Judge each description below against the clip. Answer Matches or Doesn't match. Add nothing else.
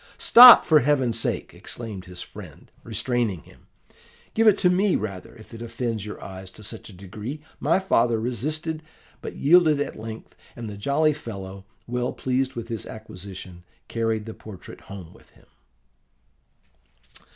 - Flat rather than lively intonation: Doesn't match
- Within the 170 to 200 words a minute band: Doesn't match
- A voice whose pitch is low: Matches